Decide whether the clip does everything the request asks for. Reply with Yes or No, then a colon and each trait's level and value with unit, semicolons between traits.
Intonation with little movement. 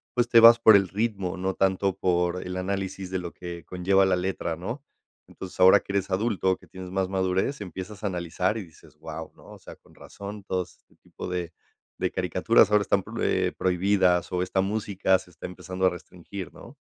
Yes: narrow, 1.7 semitones